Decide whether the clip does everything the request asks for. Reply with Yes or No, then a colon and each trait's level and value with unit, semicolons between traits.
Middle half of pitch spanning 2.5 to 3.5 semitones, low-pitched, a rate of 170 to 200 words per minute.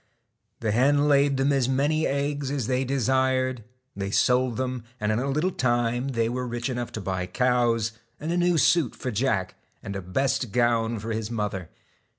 Yes: average, 3.2 semitones; low, 125 Hz; average, 180 wpm